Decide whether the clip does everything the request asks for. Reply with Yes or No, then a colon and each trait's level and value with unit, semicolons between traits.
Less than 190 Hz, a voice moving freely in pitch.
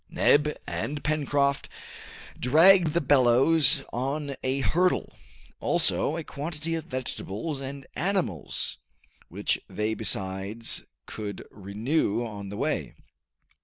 Yes: medium, 140 Hz; wide, 5.7 semitones